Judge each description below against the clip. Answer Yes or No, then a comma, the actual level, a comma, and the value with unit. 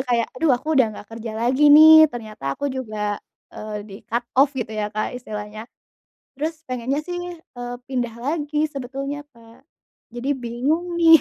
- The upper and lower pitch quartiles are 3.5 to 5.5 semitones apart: Yes, average, 4.5 semitones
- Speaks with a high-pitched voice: Yes, very high, 250 Hz